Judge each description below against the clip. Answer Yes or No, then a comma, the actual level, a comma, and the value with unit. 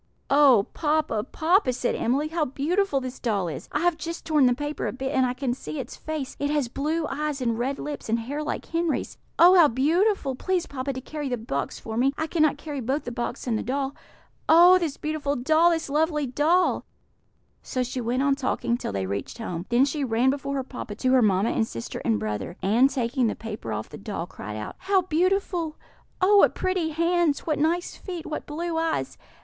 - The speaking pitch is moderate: No, very high, 280 Hz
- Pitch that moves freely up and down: No, average, 4.8 semitones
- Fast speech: Yes, fast, 215 wpm